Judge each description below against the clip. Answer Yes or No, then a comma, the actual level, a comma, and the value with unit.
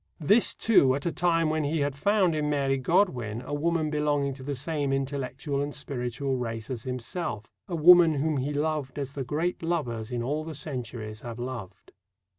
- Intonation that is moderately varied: Yes, average, 3.6 semitones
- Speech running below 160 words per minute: No, average, 190 wpm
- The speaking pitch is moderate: Yes, medium, 145 Hz